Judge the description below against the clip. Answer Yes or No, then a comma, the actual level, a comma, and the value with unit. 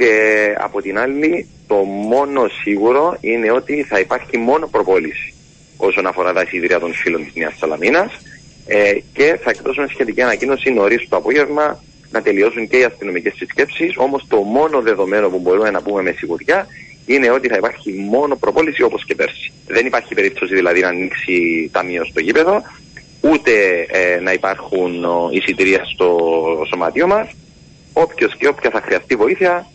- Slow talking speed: No, average, 160 wpm